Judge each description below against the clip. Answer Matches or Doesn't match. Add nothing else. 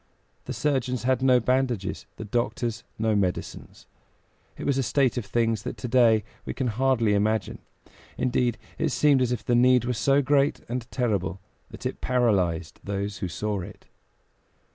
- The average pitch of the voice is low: Matches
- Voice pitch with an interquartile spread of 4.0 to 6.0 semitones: Doesn't match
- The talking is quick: Doesn't match